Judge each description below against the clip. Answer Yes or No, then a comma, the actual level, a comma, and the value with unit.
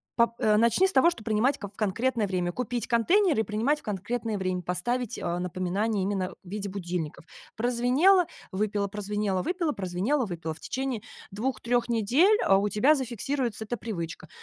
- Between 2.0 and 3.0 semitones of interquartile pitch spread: No, average, 4.5 semitones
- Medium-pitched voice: No, high, 215 Hz